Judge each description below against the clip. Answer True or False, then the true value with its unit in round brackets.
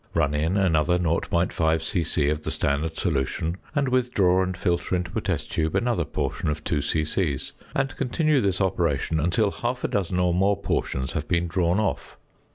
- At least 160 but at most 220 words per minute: True (175 wpm)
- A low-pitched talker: True (85 Hz)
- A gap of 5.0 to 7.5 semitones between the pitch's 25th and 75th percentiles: False (3.7 semitones)